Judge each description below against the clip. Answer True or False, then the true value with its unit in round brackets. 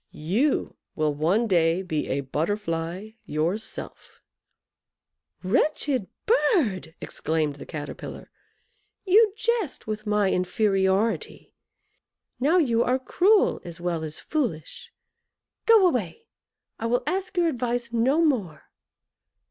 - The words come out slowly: True (110 wpm)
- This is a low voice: False (215 Hz)